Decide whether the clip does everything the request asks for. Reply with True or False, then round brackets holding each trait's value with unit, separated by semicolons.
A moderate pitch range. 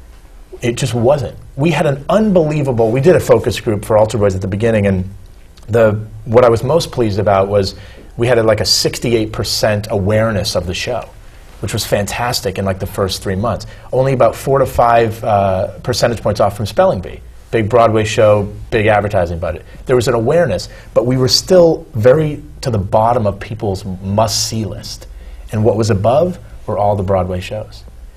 True (3.3 semitones)